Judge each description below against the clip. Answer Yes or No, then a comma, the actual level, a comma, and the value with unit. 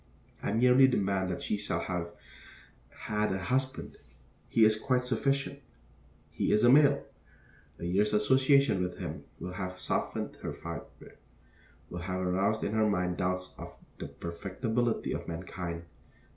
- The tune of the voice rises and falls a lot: No, average, 5.0 semitones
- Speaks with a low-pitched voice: Yes, low, 100 Hz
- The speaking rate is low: No, average, 145 wpm